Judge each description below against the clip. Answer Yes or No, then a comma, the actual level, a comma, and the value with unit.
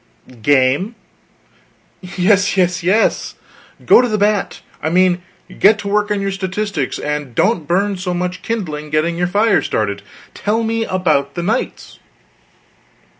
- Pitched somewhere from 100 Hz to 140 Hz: No, medium, 185 Hz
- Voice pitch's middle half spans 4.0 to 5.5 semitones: Yes, average, 4.3 semitones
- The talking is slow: No, average, 145 wpm